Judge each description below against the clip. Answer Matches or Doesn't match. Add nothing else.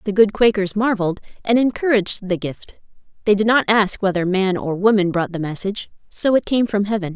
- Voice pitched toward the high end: Matches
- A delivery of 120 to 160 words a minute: Doesn't match